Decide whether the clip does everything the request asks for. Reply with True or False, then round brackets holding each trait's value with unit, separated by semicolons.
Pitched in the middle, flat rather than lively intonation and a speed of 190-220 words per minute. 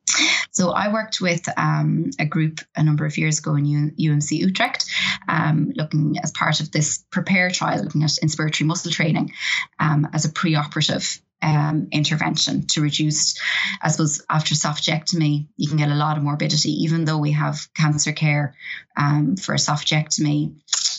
False (155 Hz; 1.4 semitones; 165 wpm)